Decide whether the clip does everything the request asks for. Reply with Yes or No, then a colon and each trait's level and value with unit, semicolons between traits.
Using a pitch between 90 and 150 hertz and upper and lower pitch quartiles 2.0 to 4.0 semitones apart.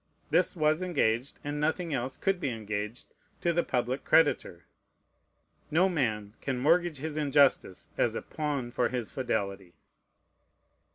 No: medium, 140 Hz; average, 4.9 semitones